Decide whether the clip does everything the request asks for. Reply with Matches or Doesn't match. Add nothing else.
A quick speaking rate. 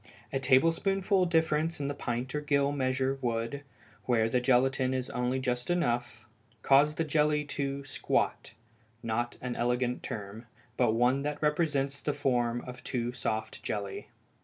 Doesn't match